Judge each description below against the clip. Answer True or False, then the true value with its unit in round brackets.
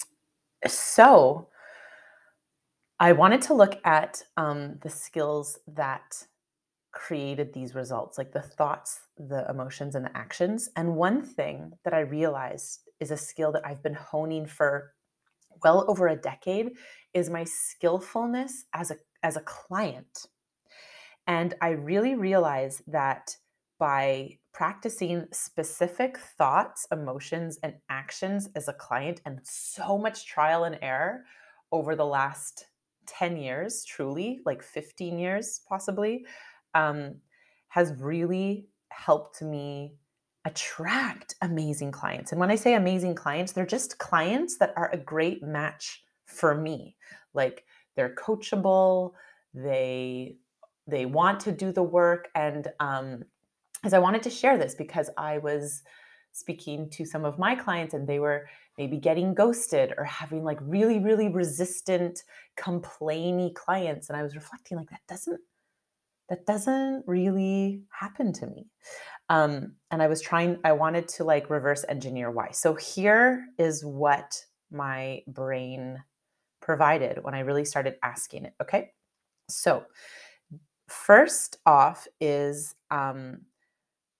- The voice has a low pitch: False (165 Hz)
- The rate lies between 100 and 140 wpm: True (135 wpm)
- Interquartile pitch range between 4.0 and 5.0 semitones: True (4.7 semitones)